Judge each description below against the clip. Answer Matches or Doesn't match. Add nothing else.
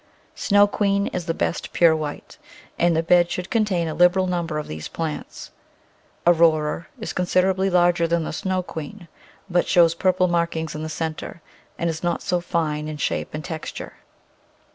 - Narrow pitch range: Matches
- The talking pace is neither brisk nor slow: Matches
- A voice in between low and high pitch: Matches